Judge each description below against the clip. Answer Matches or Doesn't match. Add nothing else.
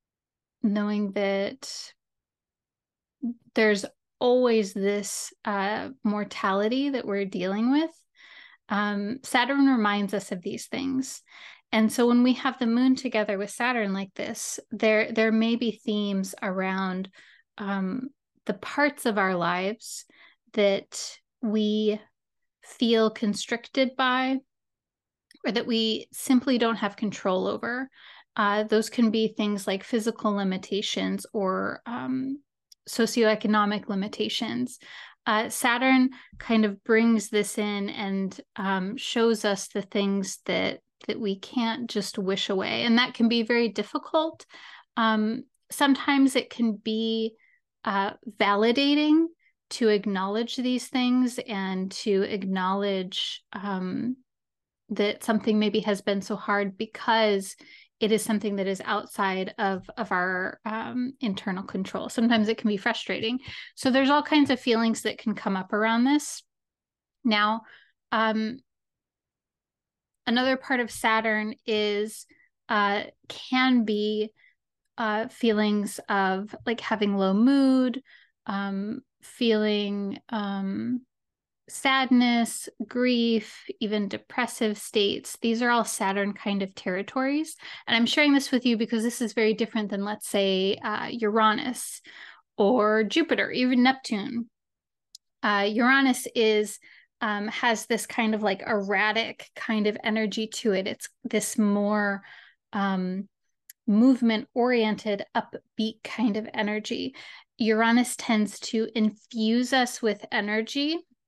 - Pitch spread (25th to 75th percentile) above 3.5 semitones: Doesn't match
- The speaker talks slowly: Matches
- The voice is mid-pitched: Doesn't match